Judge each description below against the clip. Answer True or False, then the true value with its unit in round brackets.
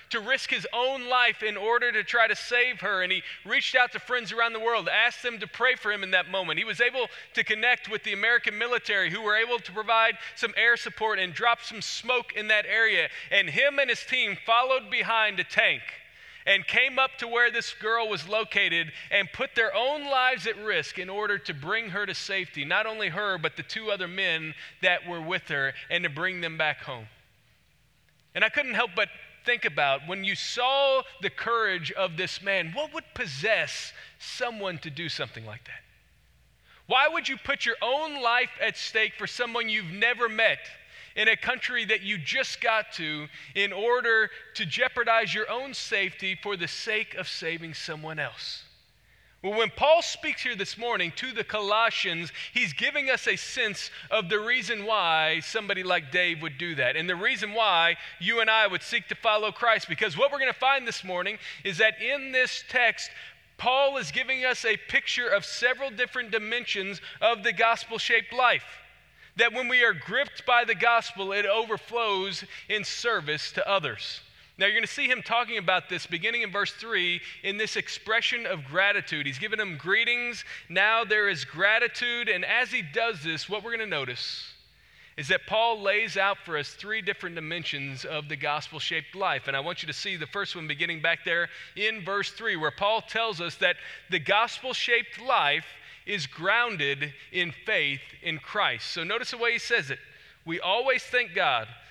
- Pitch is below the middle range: False (215 Hz)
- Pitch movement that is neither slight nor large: True (5.0 semitones)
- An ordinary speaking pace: True (195 wpm)